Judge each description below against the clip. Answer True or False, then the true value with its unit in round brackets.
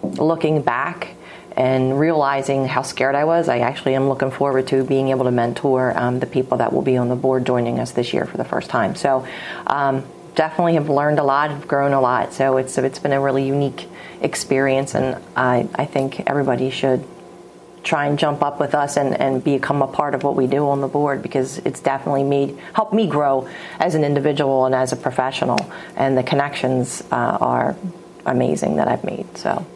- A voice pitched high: False (135 Hz)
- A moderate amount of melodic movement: False (1.8 semitones)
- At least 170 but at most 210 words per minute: True (205 wpm)